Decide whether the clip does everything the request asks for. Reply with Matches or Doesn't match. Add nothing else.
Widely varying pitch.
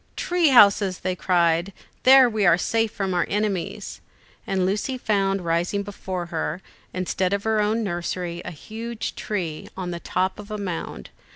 Doesn't match